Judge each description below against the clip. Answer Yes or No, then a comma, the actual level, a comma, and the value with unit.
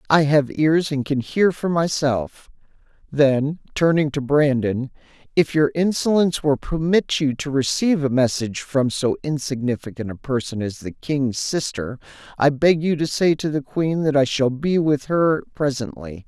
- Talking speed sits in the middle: Yes, average, 170 wpm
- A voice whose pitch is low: No, medium, 145 Hz